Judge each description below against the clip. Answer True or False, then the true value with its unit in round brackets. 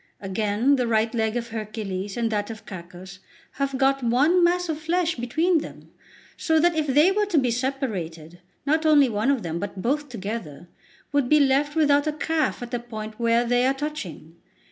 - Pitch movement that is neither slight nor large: False (5.7 semitones)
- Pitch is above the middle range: True (245 Hz)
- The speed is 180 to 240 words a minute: True (190 wpm)